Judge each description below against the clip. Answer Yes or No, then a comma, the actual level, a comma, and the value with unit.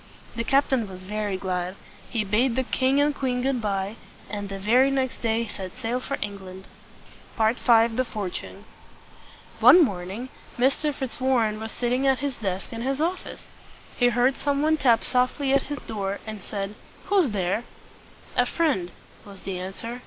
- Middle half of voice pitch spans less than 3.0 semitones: No, average, 4.8 semitones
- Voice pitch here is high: Yes, high, 235 Hz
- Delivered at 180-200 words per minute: No, average, 165 wpm